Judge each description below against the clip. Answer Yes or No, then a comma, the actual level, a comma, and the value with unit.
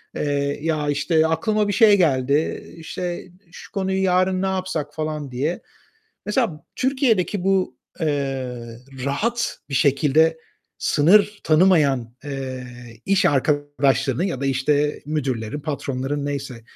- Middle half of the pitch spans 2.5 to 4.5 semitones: No, average, 5.1 semitones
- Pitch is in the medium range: Yes, medium, 150 Hz